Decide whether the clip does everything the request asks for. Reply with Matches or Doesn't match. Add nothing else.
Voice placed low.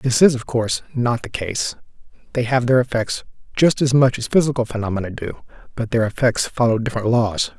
Matches